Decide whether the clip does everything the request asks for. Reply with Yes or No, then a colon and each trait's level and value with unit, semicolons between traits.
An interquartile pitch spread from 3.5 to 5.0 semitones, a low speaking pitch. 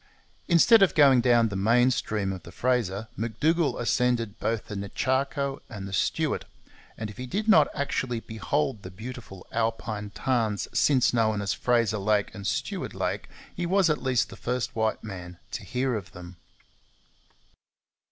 Yes: average, 4.1 semitones; low, 115 Hz